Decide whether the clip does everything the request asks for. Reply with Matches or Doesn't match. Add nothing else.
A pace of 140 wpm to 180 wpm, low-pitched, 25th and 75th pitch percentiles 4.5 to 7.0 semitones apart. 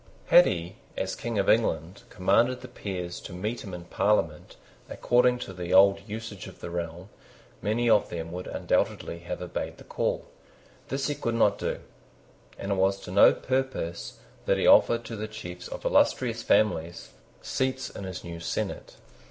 Matches